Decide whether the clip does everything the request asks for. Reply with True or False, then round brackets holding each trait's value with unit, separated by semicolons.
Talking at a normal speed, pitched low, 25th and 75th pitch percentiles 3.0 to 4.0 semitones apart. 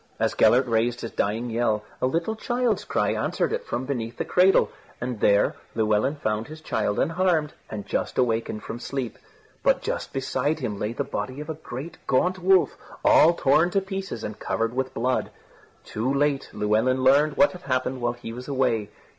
False (185 wpm; 130 Hz; 5.3 semitones)